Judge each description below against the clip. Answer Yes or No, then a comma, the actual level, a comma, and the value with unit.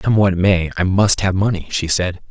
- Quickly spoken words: Yes, fast, 235 wpm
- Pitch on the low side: Yes, very low, 95 Hz